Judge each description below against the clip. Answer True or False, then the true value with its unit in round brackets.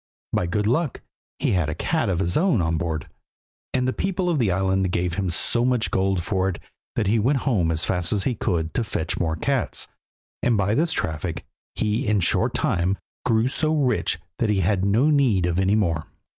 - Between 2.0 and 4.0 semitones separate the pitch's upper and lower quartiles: False (5.6 semitones)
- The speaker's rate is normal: False (210 wpm)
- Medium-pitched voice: False (100 Hz)